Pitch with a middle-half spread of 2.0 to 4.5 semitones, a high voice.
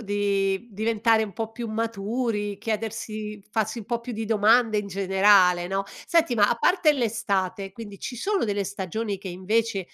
Yes: narrow, 2.5 semitones; high, 215 Hz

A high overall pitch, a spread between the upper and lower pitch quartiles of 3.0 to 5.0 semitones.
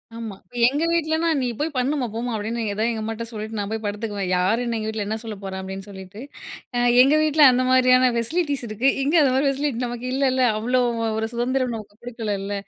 Yes: high, 235 Hz; average, 3.5 semitones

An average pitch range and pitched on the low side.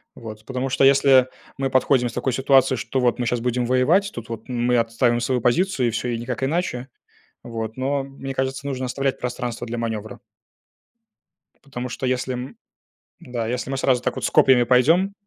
No: narrow, 1.9 semitones; low, 125 Hz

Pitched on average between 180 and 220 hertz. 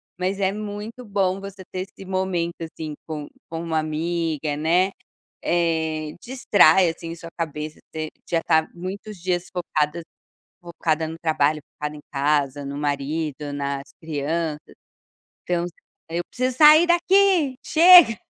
No: medium, 170 Hz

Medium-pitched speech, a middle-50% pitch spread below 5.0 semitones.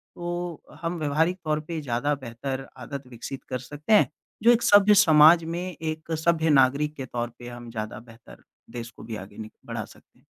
No: medium, 150 Hz; wide, 5.5 semitones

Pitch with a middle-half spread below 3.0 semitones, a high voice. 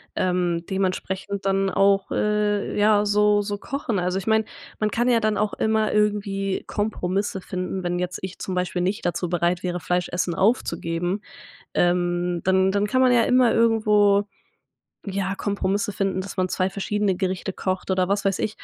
Yes: narrow, 2.4 semitones; high, 195 Hz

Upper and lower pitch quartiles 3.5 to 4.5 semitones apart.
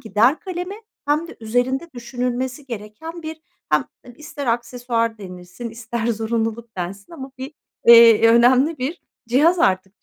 Yes: average, 4.2 semitones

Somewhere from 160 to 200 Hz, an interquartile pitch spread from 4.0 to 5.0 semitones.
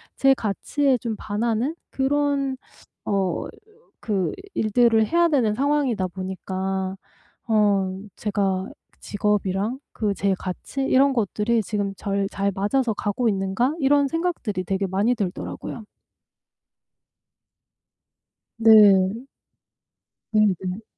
No: high, 210 Hz; average, 4.6 semitones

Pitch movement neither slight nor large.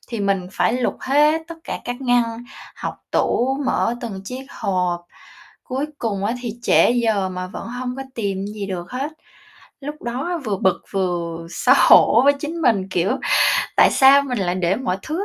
No: wide, 5.8 semitones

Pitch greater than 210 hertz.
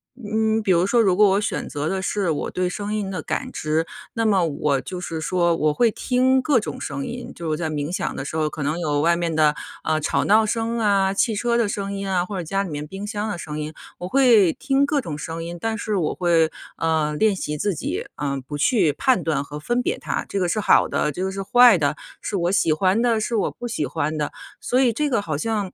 No: high, 190 Hz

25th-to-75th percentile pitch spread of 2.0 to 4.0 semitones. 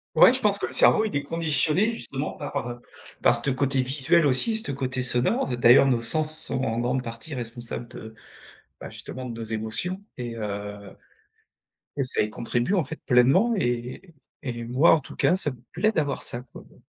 No: average, 4.6 semitones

